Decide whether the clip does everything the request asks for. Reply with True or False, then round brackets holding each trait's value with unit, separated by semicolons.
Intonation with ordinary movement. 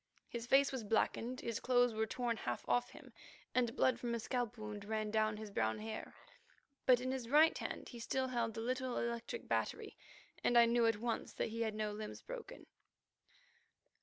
False (2.3 semitones)